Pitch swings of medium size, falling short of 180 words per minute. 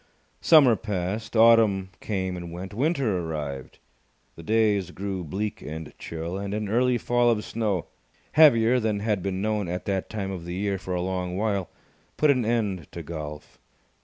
Yes: average, 3.8 semitones; average, 170 wpm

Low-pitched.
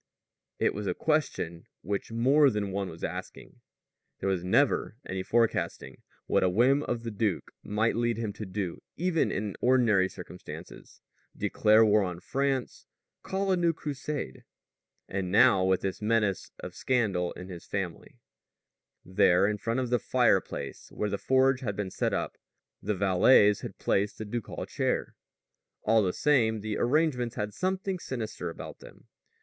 Yes: low, 110 Hz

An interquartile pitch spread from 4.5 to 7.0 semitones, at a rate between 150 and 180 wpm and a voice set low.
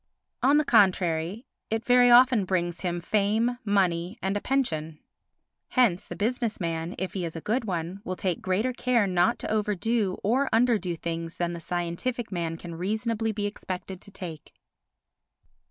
No: average, 4.8 semitones; average, 165 wpm; high, 195 Hz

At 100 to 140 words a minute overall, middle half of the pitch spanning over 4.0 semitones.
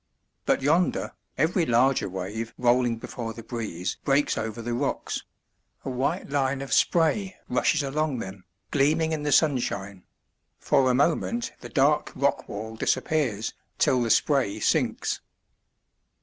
Yes: slow, 135 wpm; average, 4.6 semitones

